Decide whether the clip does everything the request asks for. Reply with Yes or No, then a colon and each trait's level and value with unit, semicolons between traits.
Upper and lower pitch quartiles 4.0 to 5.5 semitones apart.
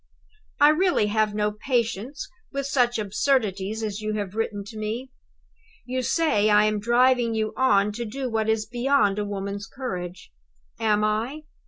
No: average, 3.5 semitones